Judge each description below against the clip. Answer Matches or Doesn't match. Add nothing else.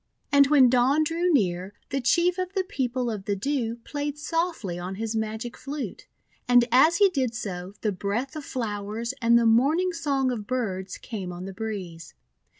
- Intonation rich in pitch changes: Matches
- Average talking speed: Matches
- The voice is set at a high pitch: Matches